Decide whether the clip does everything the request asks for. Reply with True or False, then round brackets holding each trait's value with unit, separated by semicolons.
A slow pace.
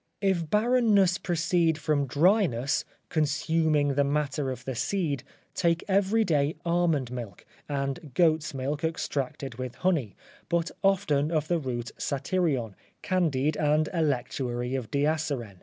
True (125 wpm)